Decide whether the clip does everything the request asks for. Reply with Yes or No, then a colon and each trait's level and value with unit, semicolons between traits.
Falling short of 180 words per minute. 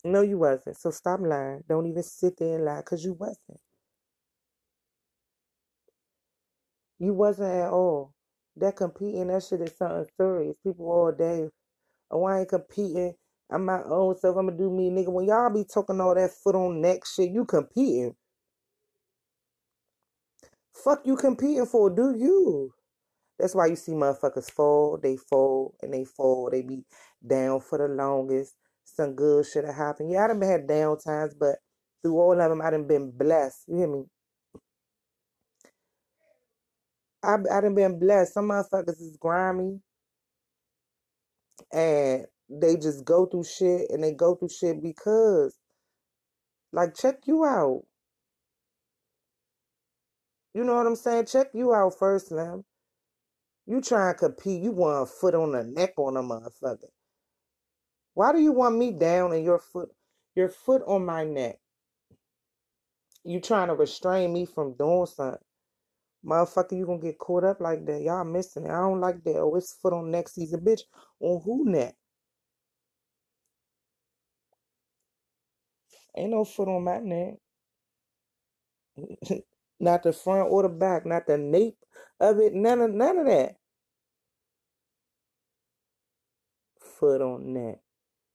Yes: average, 150 wpm